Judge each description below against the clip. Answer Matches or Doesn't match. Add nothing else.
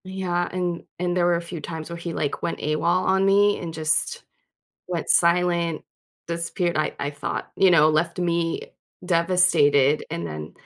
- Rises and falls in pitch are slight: Matches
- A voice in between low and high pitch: Matches